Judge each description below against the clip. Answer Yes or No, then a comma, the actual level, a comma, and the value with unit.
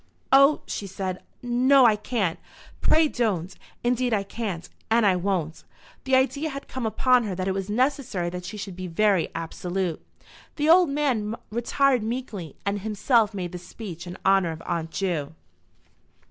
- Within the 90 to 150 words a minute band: No, average, 165 wpm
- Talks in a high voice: Yes, high, 210 Hz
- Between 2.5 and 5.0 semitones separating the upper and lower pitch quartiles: No, wide, 5.6 semitones